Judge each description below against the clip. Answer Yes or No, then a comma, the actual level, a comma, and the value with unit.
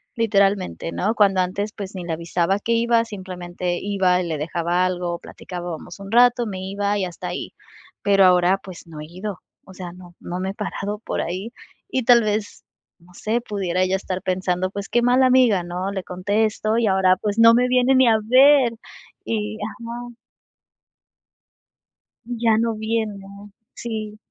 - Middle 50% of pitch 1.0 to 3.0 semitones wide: No, average, 3.7 semitones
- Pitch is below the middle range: No, high, 200 Hz